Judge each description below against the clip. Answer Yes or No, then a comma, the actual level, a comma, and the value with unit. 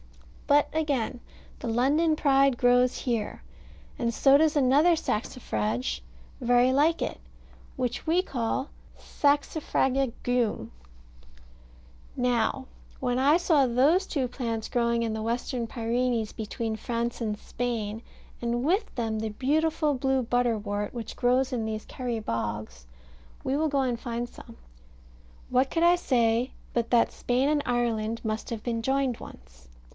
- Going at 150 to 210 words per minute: No, average, 140 wpm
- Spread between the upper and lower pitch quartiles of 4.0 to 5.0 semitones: No, average, 3.1 semitones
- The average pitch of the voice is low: No, high, 245 Hz